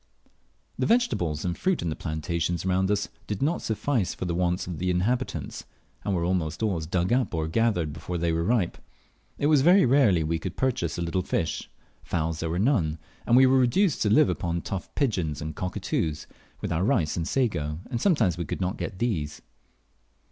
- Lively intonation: Yes, wide, 6.2 semitones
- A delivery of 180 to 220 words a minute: Yes, average, 200 wpm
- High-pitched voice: No, very low, 90 Hz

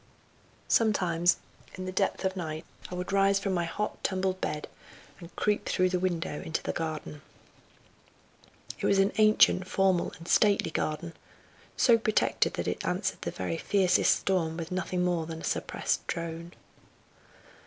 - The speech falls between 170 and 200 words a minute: No, average, 155 wpm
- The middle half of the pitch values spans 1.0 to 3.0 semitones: Yes, average, 2.7 semitones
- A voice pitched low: No, medium, 180 Hz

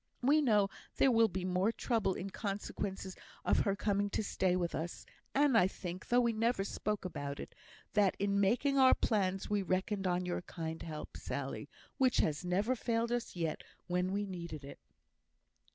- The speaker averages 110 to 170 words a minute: No, average, 180 wpm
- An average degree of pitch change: Yes, average, 4.0 semitones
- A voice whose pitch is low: No, high, 195 Hz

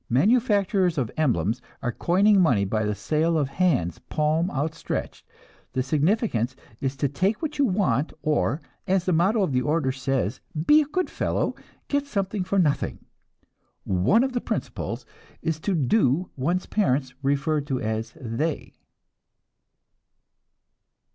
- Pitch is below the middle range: No, medium, 155 Hz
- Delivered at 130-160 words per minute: Yes, average, 140 wpm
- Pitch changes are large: Yes, wide, 6.8 semitones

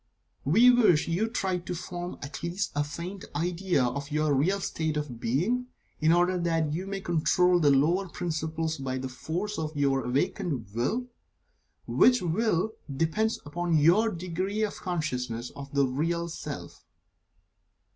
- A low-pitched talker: No, medium, 165 Hz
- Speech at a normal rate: Yes, average, 155 wpm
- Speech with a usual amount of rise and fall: Yes, average, 4.1 semitones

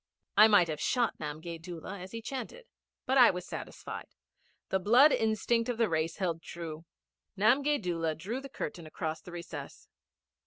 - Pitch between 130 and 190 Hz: Yes, medium, 185 Hz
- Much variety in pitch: Yes, wide, 5.9 semitones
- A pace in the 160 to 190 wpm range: Yes, average, 165 wpm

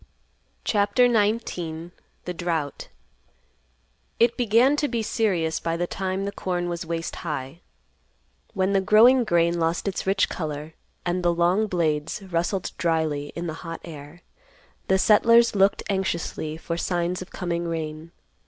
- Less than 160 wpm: Yes, average, 140 wpm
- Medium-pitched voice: Yes, medium, 175 Hz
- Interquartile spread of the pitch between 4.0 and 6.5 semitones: No, average, 3.2 semitones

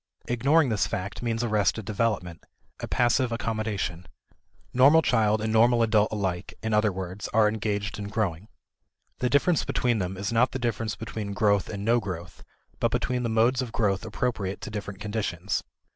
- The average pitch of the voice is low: Yes, low, 110 Hz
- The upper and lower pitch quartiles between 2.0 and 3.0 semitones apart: Yes, average, 2.7 semitones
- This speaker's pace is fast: No, average, 170 wpm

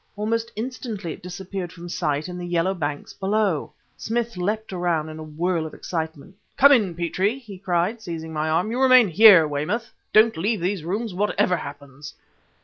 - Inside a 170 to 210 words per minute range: Yes, average, 175 wpm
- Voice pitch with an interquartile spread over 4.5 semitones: Yes, average, 5.0 semitones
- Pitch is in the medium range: Yes, medium, 180 Hz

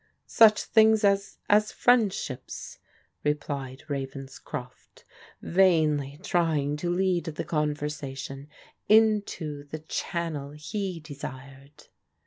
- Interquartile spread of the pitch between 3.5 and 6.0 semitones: Yes, average, 5.2 semitones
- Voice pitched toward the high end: No, medium, 150 Hz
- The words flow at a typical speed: No, slow, 105 wpm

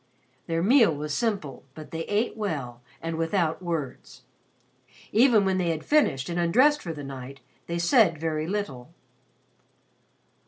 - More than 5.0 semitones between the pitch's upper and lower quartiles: Yes, wide, 5.4 semitones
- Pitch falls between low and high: Yes, medium, 165 Hz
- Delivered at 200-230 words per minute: No, average, 150 wpm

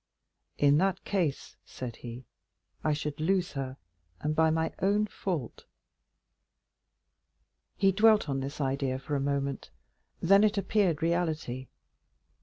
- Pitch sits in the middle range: Yes, medium, 155 Hz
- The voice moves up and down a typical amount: No, wide, 5.7 semitones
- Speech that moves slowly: Yes, slow, 125 wpm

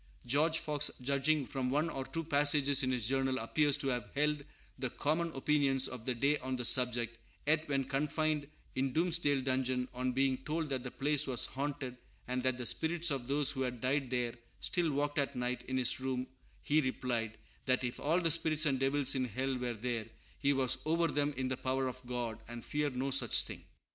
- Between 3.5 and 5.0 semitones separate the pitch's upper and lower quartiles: No, narrow, 2.5 semitones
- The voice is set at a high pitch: No, low, 135 Hz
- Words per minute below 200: No, fast, 205 wpm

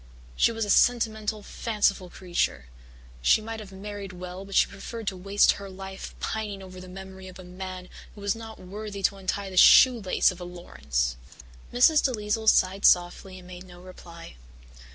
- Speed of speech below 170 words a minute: No, average, 175 wpm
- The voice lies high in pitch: Yes, high, 195 Hz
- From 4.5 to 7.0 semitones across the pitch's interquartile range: No, narrow, 2.5 semitones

